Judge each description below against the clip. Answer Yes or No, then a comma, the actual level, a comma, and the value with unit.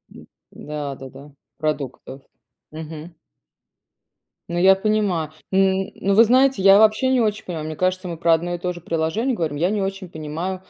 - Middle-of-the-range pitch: Yes, medium, 175 Hz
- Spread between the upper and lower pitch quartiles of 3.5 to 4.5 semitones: Yes, average, 3.8 semitones